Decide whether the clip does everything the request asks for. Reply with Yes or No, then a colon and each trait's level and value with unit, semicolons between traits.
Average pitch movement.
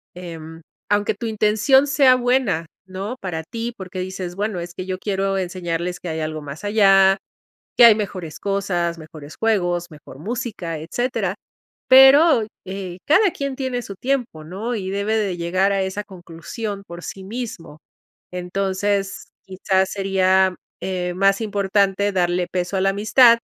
Yes: average, 3.5 semitones